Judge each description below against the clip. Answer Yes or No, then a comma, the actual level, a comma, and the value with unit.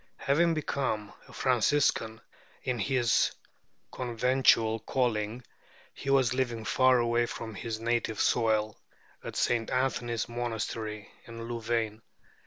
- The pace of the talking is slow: Yes, slow, 110 wpm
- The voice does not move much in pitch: Yes, narrow, 2.3 semitones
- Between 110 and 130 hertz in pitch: Yes, low, 120 Hz